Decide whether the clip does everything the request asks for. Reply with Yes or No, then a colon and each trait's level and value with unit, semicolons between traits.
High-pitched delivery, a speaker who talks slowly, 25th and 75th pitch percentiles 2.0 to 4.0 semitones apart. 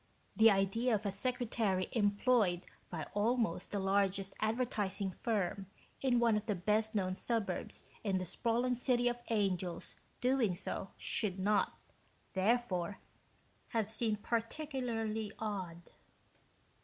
Yes: high, 210 Hz; slow, 125 wpm; average, 3.4 semitones